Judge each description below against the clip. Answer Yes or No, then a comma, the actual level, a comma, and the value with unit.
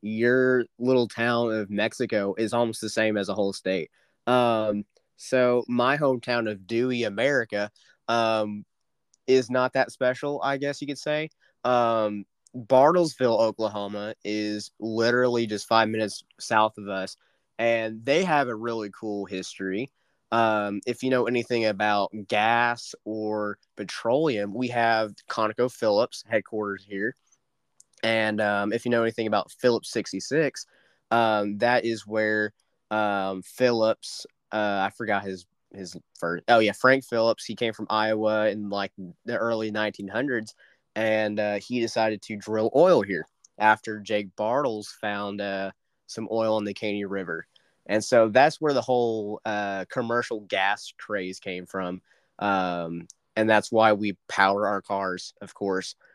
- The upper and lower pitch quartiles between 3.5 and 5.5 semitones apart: No, narrow, 2.6 semitones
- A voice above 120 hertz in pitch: No, low, 110 Hz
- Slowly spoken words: No, average, 145 wpm